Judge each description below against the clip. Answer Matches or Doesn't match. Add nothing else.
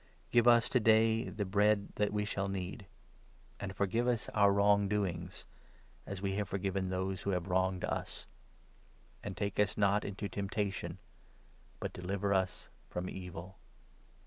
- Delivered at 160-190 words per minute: Matches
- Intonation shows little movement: Matches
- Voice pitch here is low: Matches